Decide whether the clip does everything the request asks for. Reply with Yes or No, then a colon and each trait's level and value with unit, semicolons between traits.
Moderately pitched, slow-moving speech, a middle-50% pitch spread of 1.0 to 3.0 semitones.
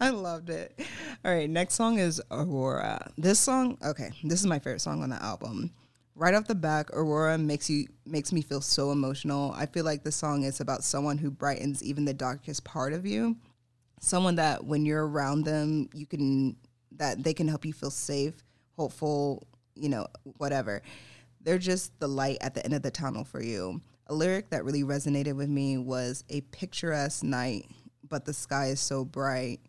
No: medium, 145 Hz; average, 195 wpm; narrow, 2.5 semitones